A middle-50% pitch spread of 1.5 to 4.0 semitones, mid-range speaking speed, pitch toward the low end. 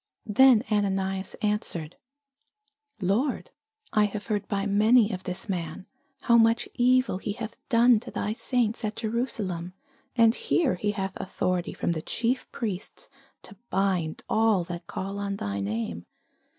No: average, 3.6 semitones; average, 145 wpm; high, 205 Hz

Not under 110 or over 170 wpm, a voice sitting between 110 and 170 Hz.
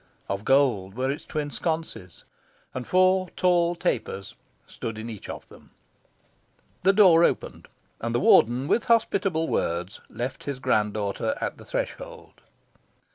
Yes: average, 140 wpm; medium, 140 Hz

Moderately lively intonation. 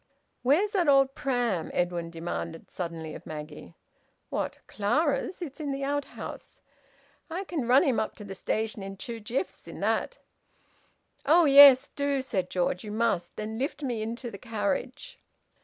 No: wide, 6.5 semitones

